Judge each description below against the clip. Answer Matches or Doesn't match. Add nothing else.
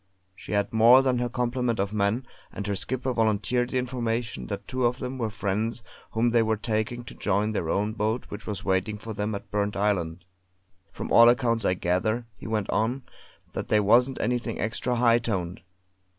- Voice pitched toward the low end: Matches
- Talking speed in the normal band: Matches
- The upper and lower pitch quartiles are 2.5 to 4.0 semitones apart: Matches